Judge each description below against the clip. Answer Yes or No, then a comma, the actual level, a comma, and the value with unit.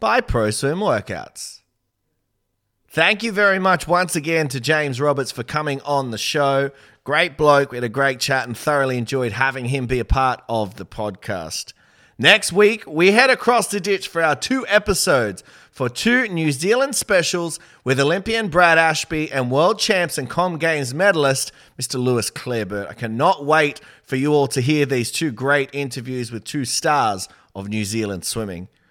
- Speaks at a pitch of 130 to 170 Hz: Yes, medium, 140 Hz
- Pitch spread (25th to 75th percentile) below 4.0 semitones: No, wide, 5.6 semitones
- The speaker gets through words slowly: No, average, 175 wpm